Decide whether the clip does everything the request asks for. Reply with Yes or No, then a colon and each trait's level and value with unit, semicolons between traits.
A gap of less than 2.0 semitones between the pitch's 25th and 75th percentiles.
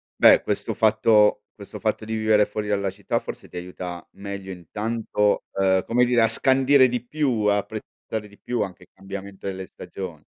No: average, 2.7 semitones